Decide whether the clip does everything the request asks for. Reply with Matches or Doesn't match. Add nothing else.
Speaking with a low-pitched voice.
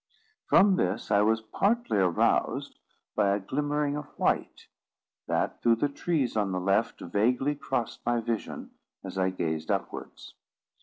Matches